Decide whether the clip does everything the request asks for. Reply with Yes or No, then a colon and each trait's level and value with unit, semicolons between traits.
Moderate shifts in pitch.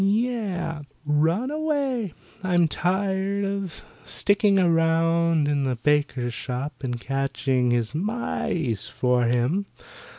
No: wide, 6.5 semitones